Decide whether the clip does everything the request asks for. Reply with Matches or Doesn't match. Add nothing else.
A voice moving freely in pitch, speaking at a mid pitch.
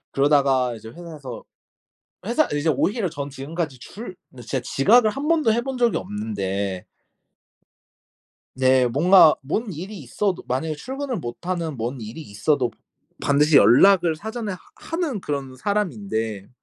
Matches